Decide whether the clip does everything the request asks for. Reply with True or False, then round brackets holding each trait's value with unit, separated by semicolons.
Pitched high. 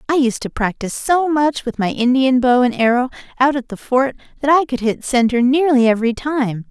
True (255 Hz)